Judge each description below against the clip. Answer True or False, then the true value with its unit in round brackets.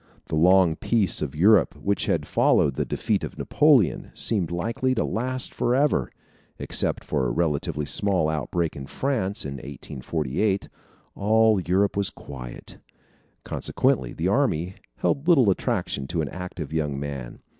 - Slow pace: False (145 wpm)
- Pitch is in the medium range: False (90 Hz)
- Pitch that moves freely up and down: True (6.9 semitones)